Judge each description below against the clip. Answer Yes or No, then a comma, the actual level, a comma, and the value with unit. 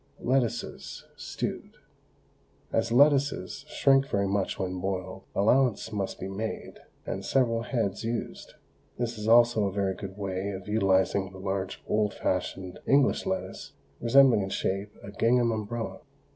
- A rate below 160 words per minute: Yes, average, 140 wpm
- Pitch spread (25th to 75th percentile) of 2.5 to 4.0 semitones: Yes, average, 3.6 semitones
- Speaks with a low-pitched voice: Yes, low, 105 Hz